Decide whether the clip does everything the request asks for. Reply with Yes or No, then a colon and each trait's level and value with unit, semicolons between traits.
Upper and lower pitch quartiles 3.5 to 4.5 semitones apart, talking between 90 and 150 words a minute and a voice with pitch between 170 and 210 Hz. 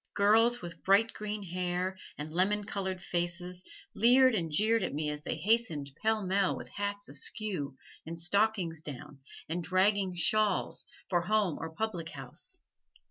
Yes: average, 4.1 semitones; average, 145 wpm; medium, 185 Hz